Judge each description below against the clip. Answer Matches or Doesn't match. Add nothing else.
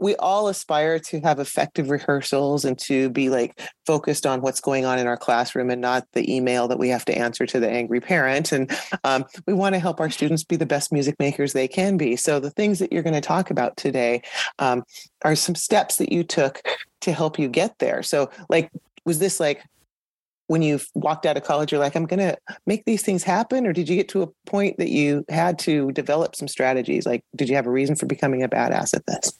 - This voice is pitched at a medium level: Matches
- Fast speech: Matches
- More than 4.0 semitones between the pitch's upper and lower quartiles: Matches